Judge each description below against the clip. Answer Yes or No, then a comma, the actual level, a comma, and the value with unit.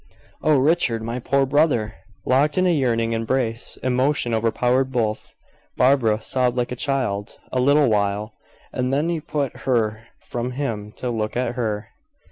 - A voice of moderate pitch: No, low, 125 Hz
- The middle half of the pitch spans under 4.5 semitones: Yes, average, 3.4 semitones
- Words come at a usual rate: Yes, average, 155 wpm